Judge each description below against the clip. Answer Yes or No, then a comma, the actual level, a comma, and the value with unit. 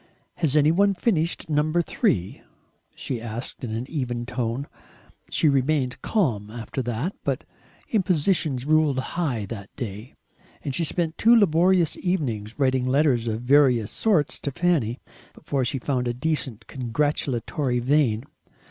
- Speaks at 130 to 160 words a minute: Yes, average, 140 wpm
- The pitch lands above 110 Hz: Yes, low, 135 Hz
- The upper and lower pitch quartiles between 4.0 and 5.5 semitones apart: Yes, average, 4.8 semitones